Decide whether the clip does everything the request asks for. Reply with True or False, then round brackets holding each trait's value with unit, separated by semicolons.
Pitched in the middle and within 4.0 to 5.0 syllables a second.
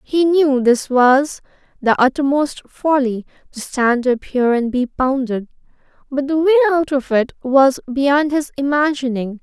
False (270 Hz; 4.2 syllables/s)